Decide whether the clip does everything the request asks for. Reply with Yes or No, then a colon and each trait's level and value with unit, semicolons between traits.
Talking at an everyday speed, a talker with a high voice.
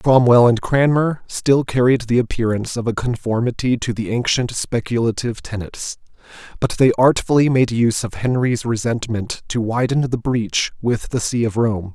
No: average, 160 wpm; low, 120 Hz